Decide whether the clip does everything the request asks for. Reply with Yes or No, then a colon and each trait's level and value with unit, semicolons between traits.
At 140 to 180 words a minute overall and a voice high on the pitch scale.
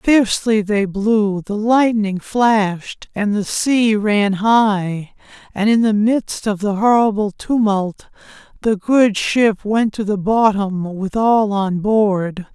Yes: average, 145 wpm; high, 210 Hz